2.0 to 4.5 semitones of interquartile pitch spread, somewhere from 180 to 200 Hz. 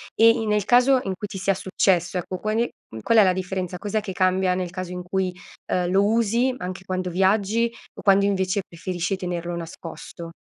Yes: narrow, 2.5 semitones; high, 190 Hz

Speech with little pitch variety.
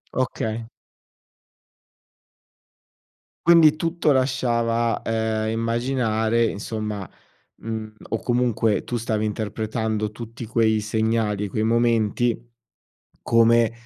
Yes: narrow, 1.4 semitones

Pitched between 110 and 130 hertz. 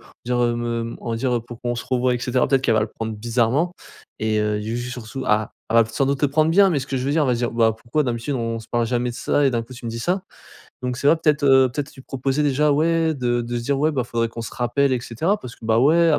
Yes: low, 125 Hz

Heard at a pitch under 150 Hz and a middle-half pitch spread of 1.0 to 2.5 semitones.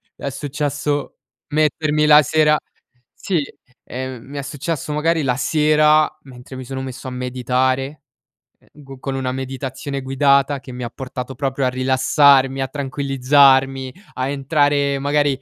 Yes: low, 135 Hz; narrow, 1.9 semitones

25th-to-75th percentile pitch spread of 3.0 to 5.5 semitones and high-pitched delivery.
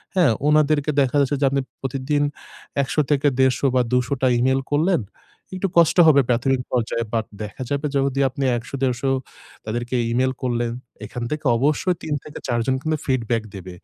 No: average, 3.3 semitones; low, 135 Hz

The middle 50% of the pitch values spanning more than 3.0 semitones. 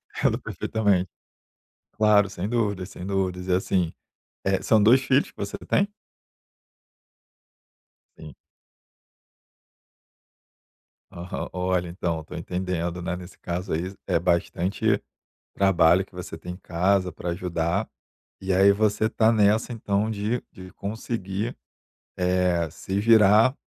No: average, 2.7 semitones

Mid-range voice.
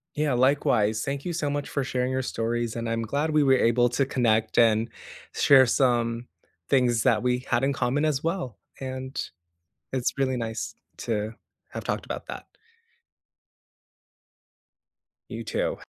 No: low, 125 Hz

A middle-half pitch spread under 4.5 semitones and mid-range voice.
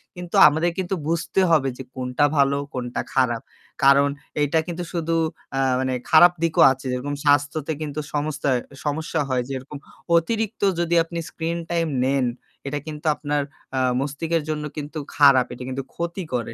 Yes: average, 3.4 semitones; medium, 150 Hz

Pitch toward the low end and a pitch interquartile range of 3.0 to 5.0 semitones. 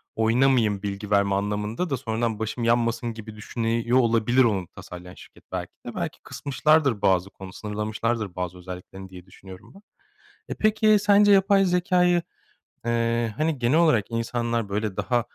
Yes: low, 115 Hz; average, 4.4 semitones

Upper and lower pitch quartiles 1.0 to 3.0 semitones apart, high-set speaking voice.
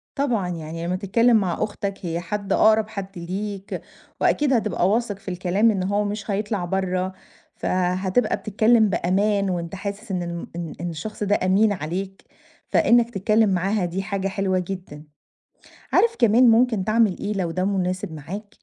Yes: average, 2.7 semitones; high, 195 Hz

